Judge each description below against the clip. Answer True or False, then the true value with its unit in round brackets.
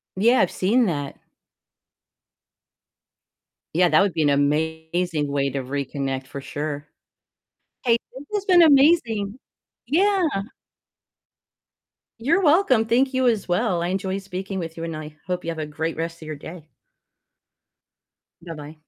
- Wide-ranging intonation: True (7.3 semitones)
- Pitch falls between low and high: True (175 Hz)